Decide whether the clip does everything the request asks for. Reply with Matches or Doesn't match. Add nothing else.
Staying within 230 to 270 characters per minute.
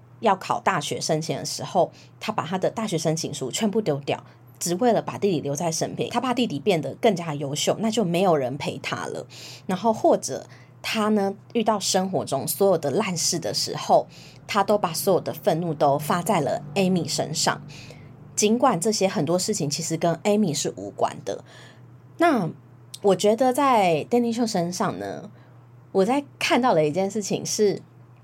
Matches